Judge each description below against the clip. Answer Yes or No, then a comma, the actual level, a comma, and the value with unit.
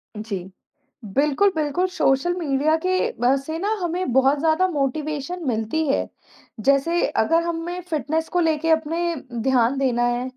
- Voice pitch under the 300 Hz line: No, very high, 305 Hz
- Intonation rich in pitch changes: No, average, 4.0 semitones